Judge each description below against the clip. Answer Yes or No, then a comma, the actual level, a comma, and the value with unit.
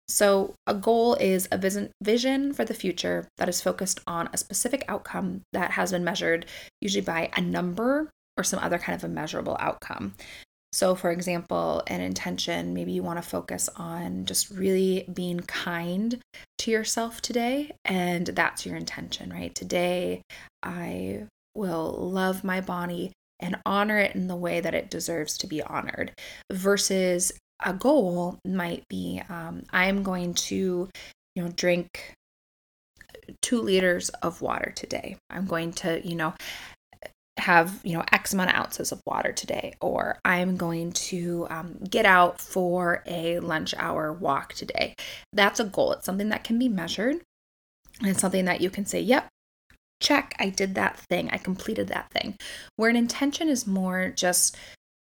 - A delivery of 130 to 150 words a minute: No, average, 160 wpm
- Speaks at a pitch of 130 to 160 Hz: No, medium, 185 Hz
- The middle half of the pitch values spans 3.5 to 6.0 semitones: No, average, 3.1 semitones